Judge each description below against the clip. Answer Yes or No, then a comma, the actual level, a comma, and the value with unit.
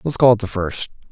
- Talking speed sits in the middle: No, fast, 270 wpm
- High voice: No, low, 110 Hz